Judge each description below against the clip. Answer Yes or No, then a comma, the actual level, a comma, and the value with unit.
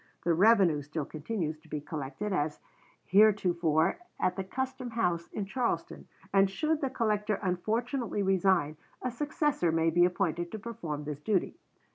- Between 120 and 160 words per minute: Yes, average, 150 wpm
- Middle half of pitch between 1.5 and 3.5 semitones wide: No, wide, 5.4 semitones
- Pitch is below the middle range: No, high, 190 Hz